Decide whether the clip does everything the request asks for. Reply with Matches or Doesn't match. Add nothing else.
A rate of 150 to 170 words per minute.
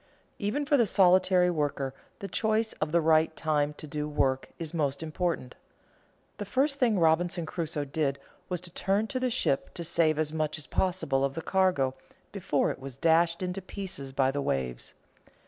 Doesn't match